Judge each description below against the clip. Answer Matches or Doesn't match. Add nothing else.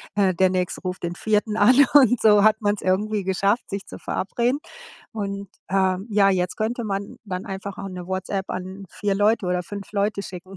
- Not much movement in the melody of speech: Matches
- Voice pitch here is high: Matches